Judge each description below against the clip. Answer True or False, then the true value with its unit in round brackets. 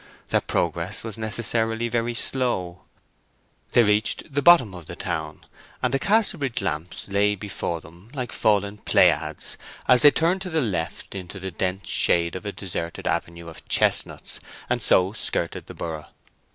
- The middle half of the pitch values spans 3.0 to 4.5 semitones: False (5.5 semitones)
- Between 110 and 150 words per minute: False (160 wpm)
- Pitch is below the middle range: True (100 Hz)